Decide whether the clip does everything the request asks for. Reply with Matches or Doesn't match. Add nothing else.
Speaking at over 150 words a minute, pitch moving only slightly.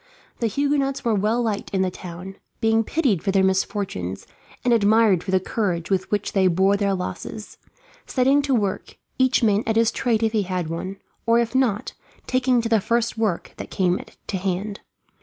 Doesn't match